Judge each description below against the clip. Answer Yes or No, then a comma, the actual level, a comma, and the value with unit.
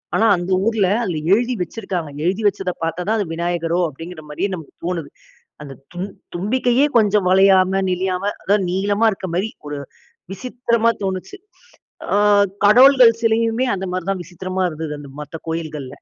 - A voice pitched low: No, high, 190 Hz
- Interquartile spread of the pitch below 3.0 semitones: No, average, 4.1 semitones